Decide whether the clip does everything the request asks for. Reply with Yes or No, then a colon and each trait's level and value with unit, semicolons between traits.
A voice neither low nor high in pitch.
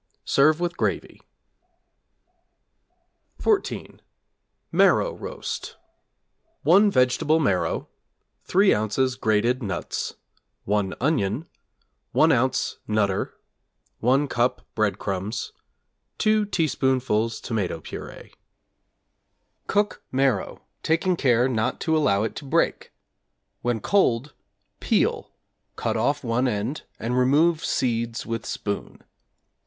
No: low, 125 Hz